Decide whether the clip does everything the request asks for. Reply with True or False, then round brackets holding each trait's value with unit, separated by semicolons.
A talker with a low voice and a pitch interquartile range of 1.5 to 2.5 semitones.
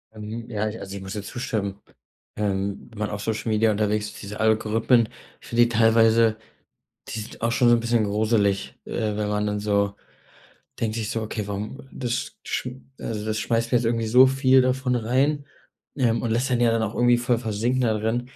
True (110 Hz; 2.2 semitones)